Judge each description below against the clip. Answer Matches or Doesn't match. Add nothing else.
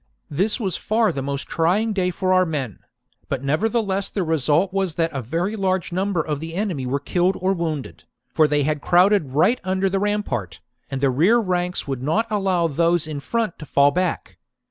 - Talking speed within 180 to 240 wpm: Matches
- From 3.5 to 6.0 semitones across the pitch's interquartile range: Matches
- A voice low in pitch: Doesn't match